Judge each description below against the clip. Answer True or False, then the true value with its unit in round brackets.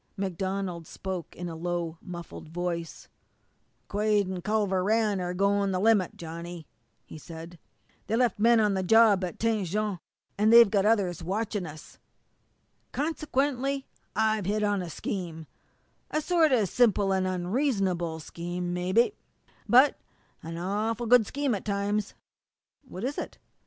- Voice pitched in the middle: False (200 Hz)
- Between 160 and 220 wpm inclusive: False (145 wpm)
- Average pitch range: True (4.0 semitones)